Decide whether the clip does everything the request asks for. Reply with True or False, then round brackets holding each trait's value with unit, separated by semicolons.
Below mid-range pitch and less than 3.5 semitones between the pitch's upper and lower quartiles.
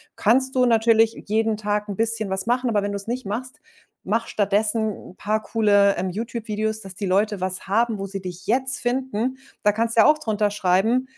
False (220 Hz; 2.5 semitones)